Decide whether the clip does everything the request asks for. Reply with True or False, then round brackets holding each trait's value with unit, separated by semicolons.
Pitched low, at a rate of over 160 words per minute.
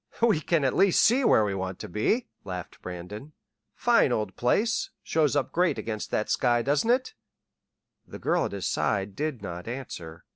True (120 Hz; 180 wpm)